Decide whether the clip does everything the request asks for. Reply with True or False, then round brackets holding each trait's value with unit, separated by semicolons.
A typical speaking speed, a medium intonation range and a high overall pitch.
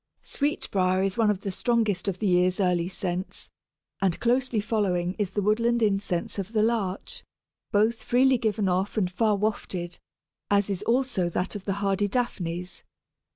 True (160 wpm; 3.3 semitones; 200 Hz)